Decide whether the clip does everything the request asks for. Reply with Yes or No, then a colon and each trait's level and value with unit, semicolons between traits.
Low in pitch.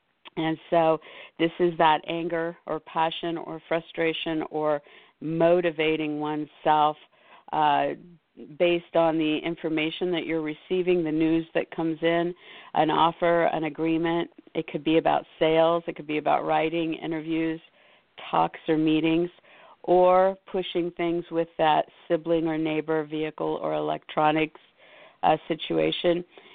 No: medium, 165 Hz